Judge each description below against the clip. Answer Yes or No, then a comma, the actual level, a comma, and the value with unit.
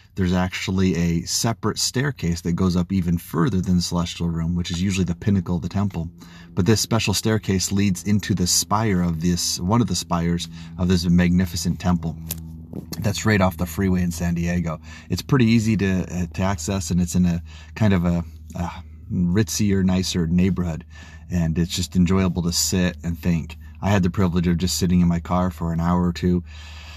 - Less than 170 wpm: No, fast, 205 wpm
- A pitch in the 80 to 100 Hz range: Yes, very low, 90 Hz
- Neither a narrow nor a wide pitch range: No, narrow, 2.0 semitones